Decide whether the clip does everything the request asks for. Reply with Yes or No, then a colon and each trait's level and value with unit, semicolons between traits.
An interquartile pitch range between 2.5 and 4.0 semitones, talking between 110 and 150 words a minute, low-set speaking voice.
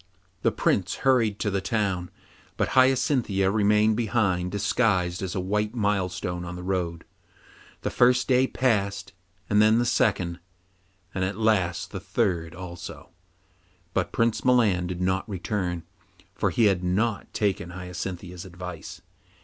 Yes: average, 3.4 semitones; average, 140 wpm; very low, 95 Hz